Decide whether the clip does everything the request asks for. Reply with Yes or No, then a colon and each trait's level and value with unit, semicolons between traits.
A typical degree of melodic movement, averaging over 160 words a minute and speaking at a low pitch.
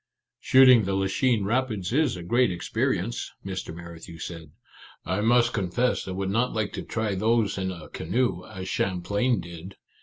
Yes: average, 4.7 semitones; average, 175 wpm; low, 100 Hz